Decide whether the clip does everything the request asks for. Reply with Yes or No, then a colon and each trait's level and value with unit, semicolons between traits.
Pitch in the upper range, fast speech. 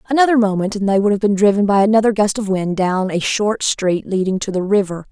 Yes: high, 205 Hz; fast, 245 wpm